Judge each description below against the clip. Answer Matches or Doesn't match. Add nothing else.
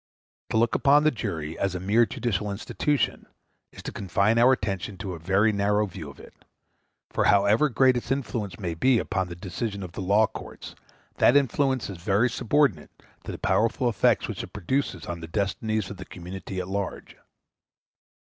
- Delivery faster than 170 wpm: Matches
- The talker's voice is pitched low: Matches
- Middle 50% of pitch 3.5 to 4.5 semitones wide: Matches